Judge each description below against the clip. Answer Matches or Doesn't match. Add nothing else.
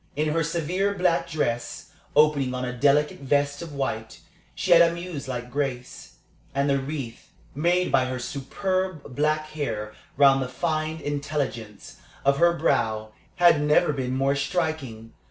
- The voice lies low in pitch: Doesn't match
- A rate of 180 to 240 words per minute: Doesn't match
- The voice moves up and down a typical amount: Matches